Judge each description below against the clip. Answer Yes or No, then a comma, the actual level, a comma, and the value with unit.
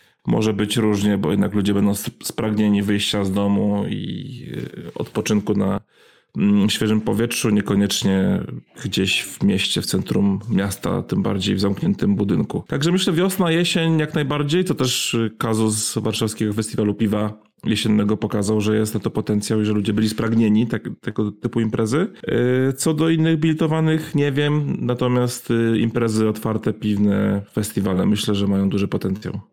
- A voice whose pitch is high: No, low, 110 Hz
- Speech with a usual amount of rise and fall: Yes, average, 3.0 semitones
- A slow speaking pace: No, average, 145 wpm